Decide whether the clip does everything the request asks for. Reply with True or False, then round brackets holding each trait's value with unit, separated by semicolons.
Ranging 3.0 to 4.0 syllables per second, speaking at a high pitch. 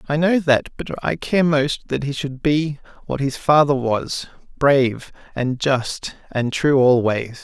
False (3.9 syllables/s; 140 Hz)